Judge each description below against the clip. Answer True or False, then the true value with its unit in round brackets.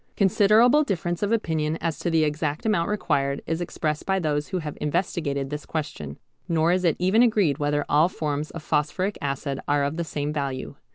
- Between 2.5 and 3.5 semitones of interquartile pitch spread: False (3.9 semitones)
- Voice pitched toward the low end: False (160 Hz)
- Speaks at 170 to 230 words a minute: True (190 wpm)